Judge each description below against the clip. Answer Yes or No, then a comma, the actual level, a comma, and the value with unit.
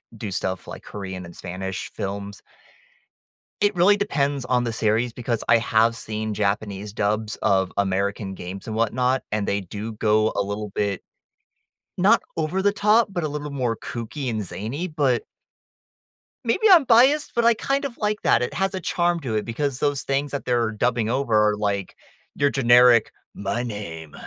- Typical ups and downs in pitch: No, wide, 6.1 semitones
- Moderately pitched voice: No, low, 115 Hz